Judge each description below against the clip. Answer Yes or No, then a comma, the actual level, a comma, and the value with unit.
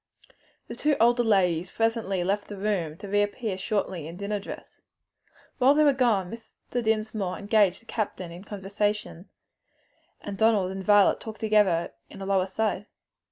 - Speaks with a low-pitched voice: No, high, 205 Hz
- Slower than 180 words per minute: Yes, average, 160 wpm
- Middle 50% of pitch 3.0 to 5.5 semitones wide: No, narrow, 2.6 semitones